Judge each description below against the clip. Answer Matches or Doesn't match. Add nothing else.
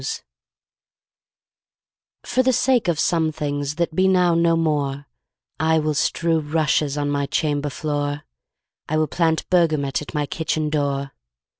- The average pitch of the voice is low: Doesn't match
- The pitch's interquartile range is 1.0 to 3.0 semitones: Matches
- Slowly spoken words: Doesn't match